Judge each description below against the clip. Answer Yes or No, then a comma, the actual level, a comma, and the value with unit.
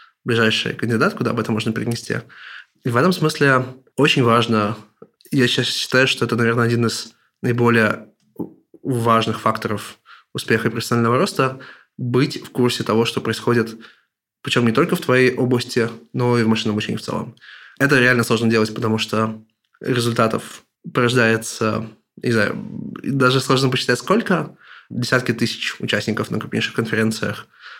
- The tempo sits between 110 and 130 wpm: No, average, 145 wpm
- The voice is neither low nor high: No, low, 120 Hz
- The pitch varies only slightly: Yes, narrow, 2.2 semitones